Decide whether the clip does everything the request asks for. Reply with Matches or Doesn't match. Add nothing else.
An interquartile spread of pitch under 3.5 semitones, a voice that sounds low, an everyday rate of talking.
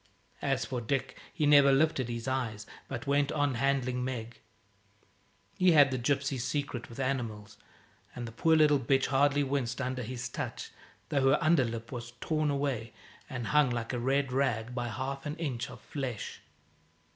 Matches